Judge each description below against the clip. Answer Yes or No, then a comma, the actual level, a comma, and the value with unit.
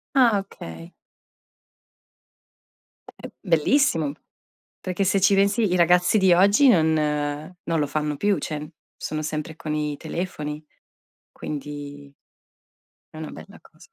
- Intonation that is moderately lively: Yes, average, 4.3 semitones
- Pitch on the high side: No, medium, 160 Hz